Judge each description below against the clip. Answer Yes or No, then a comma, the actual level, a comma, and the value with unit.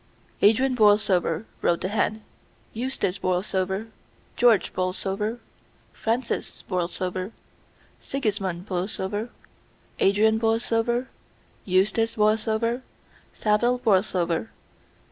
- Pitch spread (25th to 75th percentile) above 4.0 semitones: No, average, 3.3 semitones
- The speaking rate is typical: No, slow, 75 wpm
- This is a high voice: Yes, high, 210 Hz